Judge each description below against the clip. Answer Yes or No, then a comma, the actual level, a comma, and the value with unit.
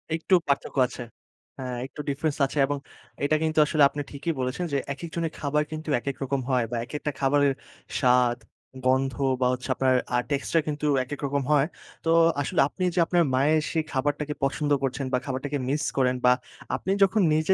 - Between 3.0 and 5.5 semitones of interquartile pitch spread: No, narrow, 2.5 semitones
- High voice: No, medium, 140 Hz